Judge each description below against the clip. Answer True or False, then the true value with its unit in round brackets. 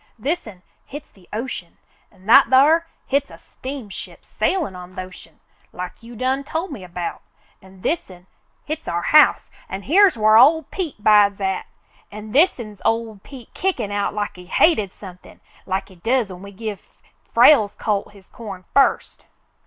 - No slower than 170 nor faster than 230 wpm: False (160 wpm)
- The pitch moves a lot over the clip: True (6.2 semitones)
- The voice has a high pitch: True (215 Hz)